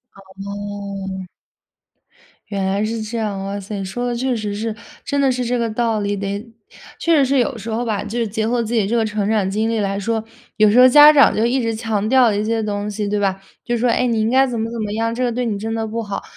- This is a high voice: Yes, high, 220 Hz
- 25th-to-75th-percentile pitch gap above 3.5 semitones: No, average, 2.7 semitones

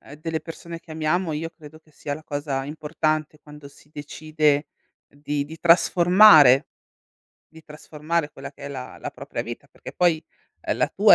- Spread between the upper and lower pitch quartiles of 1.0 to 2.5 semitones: Yes, narrow, 1.9 semitones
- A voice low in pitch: No, medium, 155 Hz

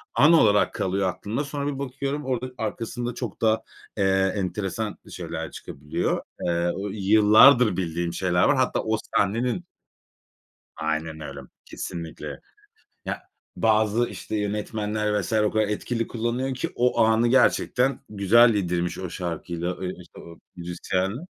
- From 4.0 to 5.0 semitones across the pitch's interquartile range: Yes, average, 4.7 semitones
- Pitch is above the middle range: No, low, 105 Hz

